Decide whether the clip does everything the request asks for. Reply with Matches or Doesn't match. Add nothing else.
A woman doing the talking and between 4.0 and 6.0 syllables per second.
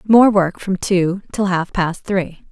Doesn't match